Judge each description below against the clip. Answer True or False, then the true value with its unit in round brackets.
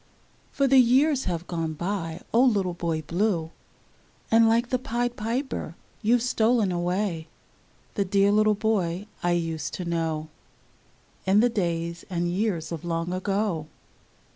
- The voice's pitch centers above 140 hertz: True (190 Hz)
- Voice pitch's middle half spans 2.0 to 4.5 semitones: False (4.9 semitones)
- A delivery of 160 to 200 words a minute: False (145 wpm)